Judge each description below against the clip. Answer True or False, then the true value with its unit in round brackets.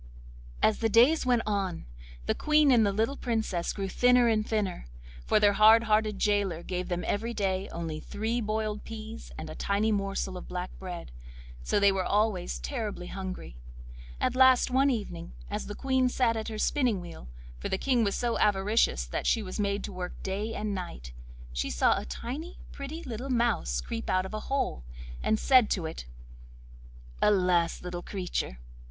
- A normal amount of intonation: True (4.2 semitones)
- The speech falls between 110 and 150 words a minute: False (175 wpm)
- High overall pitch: True (205 Hz)